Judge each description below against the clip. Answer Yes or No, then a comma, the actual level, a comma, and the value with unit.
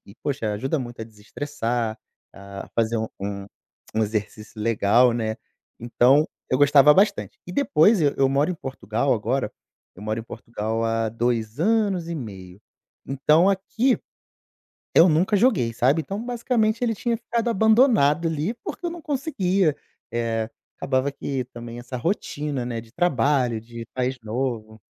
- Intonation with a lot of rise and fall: Yes, wide, 7.6 semitones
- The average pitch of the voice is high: No, low, 130 Hz